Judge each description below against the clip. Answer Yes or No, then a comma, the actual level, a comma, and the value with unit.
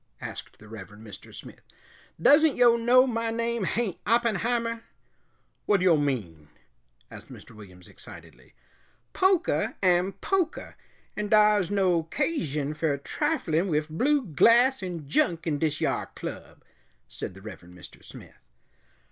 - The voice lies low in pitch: No, medium, 185 Hz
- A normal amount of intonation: No, wide, 8.2 semitones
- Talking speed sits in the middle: No, slow, 130 wpm